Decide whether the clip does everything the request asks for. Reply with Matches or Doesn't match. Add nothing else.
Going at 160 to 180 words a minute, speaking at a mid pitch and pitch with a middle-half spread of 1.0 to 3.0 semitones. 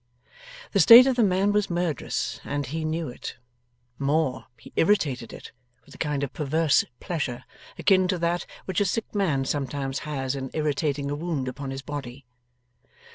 Doesn't match